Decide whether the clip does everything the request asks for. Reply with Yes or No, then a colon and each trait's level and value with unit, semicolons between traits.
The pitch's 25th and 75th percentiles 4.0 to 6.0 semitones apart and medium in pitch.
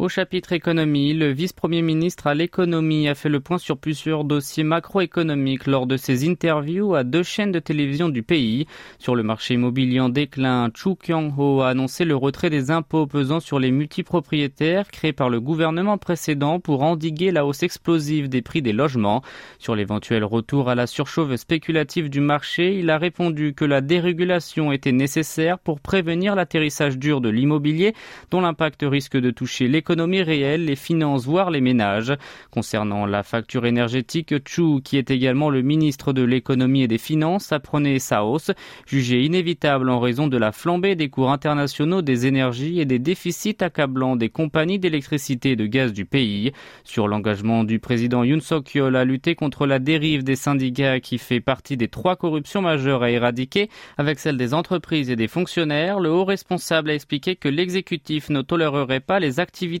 Yes: average, 4.3 semitones; medium, 150 Hz